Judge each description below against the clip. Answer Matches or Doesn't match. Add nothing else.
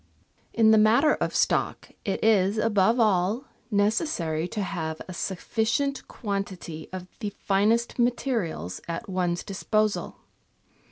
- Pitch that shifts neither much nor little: Matches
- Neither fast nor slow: Doesn't match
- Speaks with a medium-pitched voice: Doesn't match